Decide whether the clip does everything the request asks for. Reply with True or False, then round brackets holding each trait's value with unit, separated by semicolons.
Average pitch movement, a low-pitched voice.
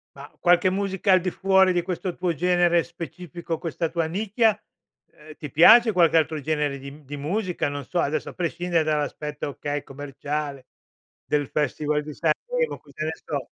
False (3.5 semitones; 165 Hz)